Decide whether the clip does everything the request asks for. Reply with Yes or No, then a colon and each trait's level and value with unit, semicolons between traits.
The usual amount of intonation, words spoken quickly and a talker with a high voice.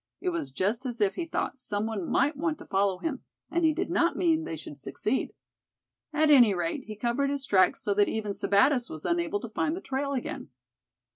No: wide, 6.8 semitones; fast, 215 wpm; high, 235 Hz